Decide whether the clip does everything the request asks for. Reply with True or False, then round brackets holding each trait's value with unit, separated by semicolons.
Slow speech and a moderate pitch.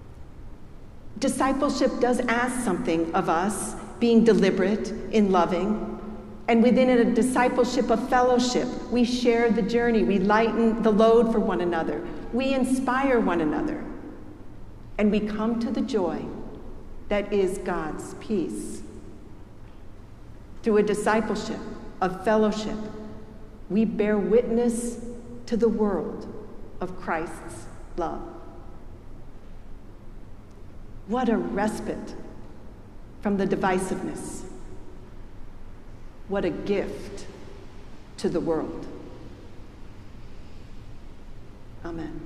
False (95 wpm; 210 Hz)